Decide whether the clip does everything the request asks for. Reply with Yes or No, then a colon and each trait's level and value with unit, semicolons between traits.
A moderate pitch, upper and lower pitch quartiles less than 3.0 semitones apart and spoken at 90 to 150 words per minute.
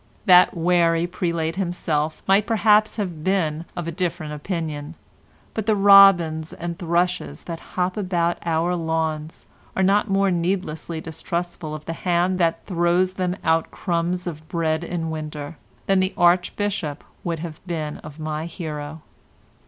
Yes: medium, 170 Hz; narrow, 2.4 semitones; average, 145 wpm